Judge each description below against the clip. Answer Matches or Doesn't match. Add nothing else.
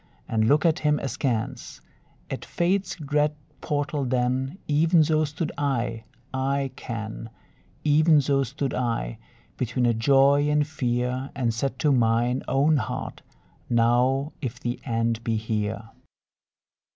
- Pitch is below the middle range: Matches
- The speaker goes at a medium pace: Doesn't match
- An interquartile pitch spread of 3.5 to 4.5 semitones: Matches